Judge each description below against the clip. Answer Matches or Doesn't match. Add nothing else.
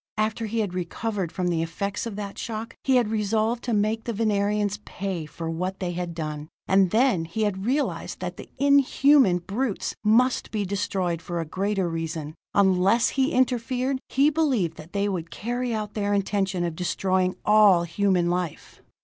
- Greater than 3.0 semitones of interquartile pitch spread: Matches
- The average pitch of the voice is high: Matches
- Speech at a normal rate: Matches